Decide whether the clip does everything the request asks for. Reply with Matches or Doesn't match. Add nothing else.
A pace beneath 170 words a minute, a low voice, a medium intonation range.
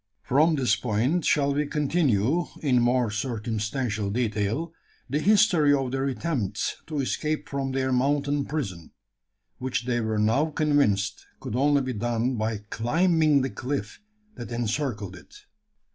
Matches